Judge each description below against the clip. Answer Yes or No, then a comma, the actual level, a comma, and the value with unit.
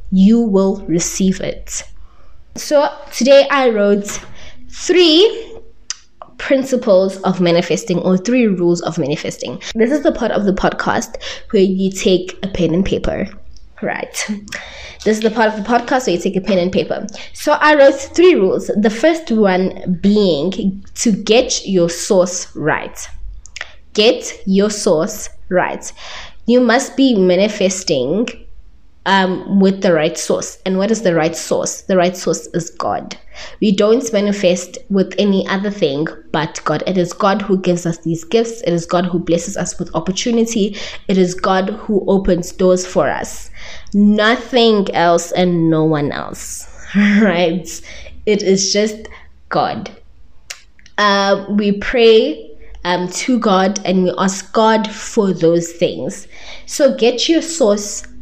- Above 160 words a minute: No, average, 150 wpm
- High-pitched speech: Yes, high, 195 Hz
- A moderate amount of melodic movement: Yes, average, 3.8 semitones